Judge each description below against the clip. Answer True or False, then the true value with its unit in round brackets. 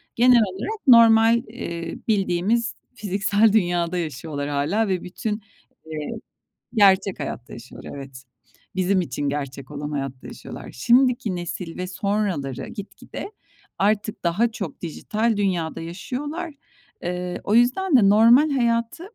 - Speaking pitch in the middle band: False (195 Hz)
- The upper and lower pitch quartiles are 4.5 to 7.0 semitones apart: True (5.4 semitones)